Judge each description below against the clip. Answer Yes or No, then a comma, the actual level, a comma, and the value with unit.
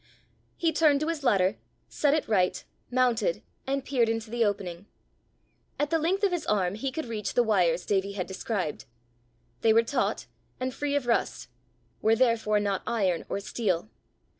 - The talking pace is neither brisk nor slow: Yes, average, 170 wpm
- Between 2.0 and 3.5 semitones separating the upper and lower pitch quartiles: No, wide, 5.6 semitones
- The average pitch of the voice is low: No, high, 225 Hz